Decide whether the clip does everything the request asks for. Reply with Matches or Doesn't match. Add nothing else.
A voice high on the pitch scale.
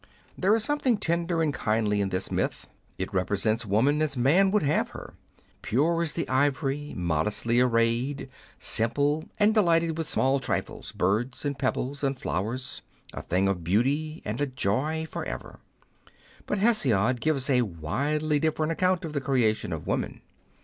Doesn't match